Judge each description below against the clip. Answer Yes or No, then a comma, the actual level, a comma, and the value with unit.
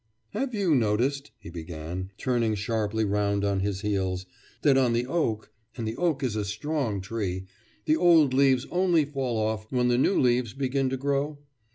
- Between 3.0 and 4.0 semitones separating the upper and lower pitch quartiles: No, average, 5.2 semitones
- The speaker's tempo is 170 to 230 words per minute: Yes, average, 180 wpm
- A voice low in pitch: Yes, low, 120 Hz